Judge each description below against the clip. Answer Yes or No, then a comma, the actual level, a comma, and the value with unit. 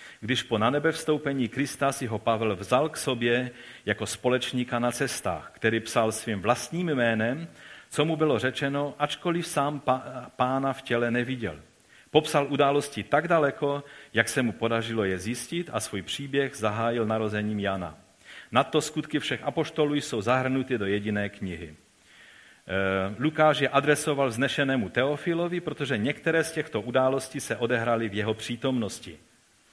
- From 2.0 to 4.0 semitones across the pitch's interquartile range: No, average, 4.4 semitones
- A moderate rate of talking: Yes, average, 145 wpm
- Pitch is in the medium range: No, low, 130 Hz